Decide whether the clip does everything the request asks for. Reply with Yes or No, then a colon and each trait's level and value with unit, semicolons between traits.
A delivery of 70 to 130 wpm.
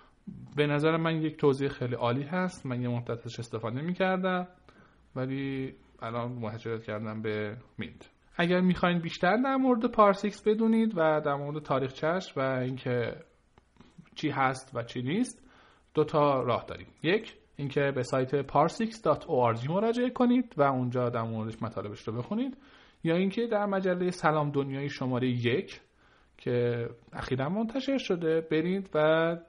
No: average, 140 wpm